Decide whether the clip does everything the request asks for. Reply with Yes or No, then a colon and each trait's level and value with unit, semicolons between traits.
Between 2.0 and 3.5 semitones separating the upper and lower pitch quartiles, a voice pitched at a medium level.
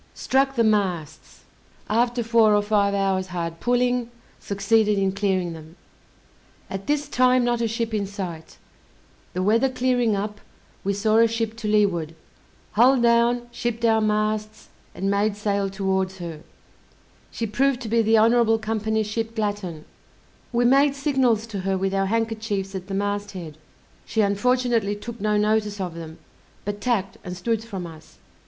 No: average, 3.1 semitones; high, 210 Hz